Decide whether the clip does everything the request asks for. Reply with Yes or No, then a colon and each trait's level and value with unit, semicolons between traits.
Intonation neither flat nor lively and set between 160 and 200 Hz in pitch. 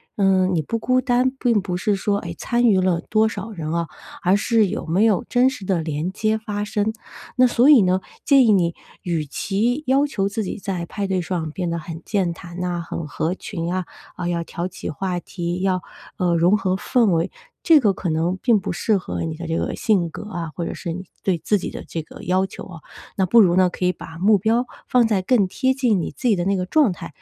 Yes: average, 3.9 semitones; high, 190 Hz